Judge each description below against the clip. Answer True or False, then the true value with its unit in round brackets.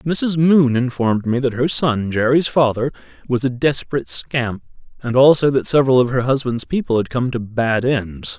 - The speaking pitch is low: True (125 Hz)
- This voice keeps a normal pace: True (170 wpm)